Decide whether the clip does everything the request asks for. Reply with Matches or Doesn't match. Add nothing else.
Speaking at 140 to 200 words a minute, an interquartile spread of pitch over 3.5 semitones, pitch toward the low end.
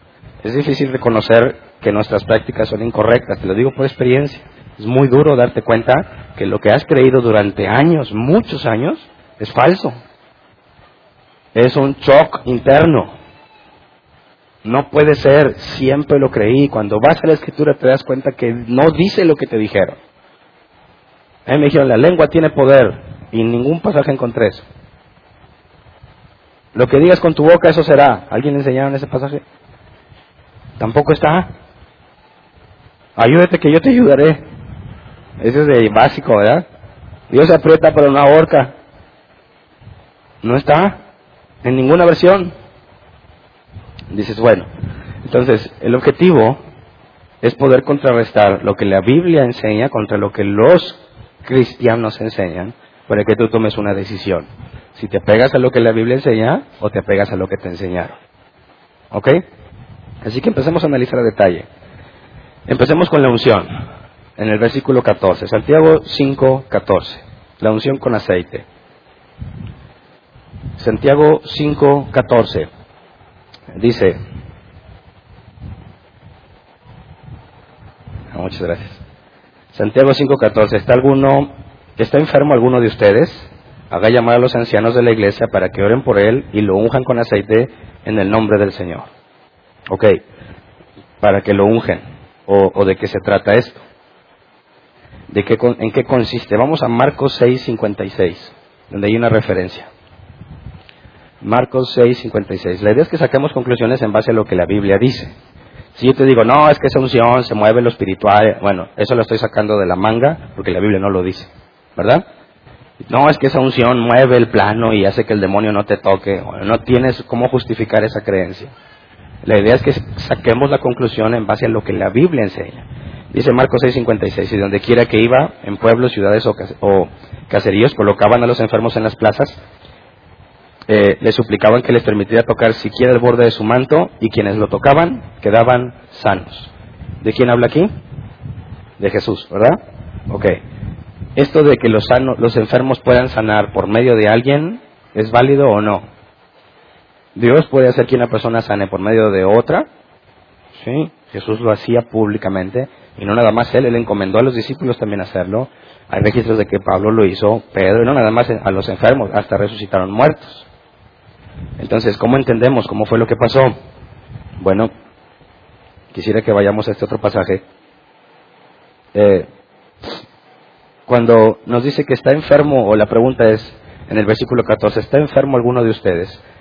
Matches